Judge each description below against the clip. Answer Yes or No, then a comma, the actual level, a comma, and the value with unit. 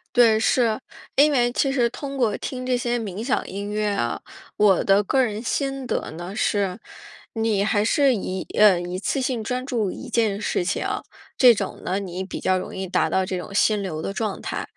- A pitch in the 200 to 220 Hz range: Yes, high, 215 Hz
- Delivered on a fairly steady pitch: No, average, 4.1 semitones